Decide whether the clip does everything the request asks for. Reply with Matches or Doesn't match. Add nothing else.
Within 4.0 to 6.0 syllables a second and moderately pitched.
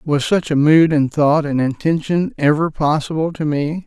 Matches